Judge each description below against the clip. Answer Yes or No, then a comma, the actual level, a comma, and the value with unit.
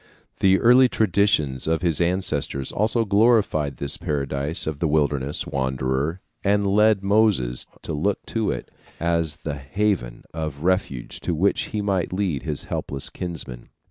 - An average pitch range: No, wide, 6.1 semitones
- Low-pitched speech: Yes, very low, 85 Hz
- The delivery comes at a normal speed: Yes, average, 145 wpm